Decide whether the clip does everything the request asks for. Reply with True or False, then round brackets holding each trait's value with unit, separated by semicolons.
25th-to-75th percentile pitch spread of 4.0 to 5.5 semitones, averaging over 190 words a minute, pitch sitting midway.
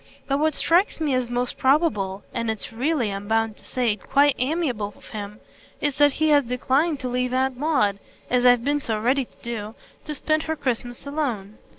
False (4.5 semitones; 200 wpm; 250 Hz)